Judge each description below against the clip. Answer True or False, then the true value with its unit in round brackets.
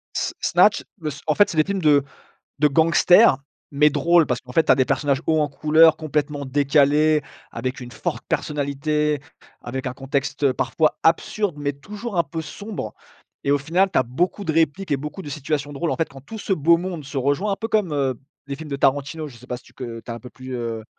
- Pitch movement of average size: True (3.1 semitones)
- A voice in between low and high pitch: True (150 Hz)